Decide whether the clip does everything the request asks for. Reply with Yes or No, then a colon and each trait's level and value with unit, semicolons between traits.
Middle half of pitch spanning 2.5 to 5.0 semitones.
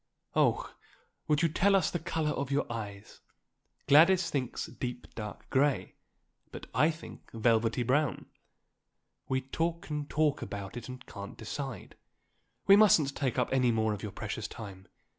No: wide, 5.5 semitones